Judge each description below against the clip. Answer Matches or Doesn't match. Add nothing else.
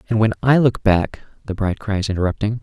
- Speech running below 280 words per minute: Matches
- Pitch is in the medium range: Doesn't match